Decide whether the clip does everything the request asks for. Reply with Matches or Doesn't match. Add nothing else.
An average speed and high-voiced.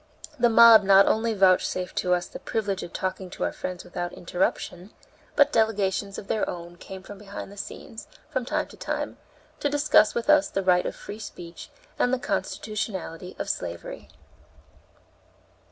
Matches